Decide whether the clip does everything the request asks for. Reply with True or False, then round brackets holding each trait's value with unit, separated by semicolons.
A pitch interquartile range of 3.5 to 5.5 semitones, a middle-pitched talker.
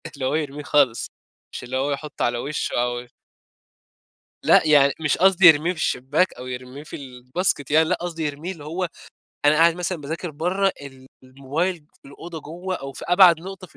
True (4.2 semitones; 150 Hz)